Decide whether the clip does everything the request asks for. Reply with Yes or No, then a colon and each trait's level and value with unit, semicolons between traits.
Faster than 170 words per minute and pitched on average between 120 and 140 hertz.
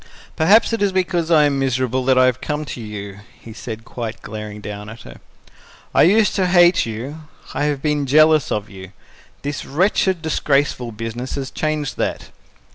Yes: average, 180 wpm; low, 135 Hz